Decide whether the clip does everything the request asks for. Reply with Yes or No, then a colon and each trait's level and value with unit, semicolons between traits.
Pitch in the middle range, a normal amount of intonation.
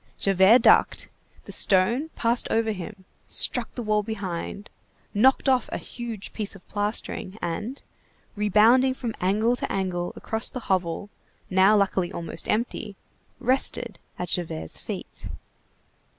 No: high, 210 Hz; average, 3.8 semitones